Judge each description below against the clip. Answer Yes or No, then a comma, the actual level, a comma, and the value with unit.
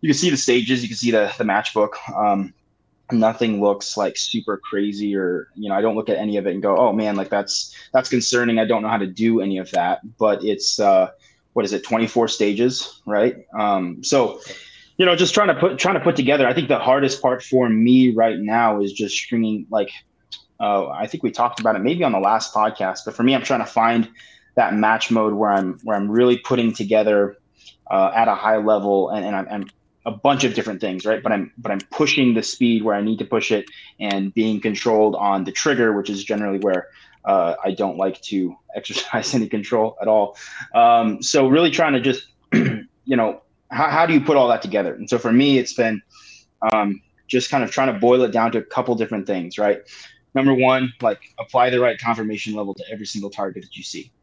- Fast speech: Yes, fast, 230 wpm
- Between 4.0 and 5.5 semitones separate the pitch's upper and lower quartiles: No, average, 3.2 semitones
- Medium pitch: No, low, 110 Hz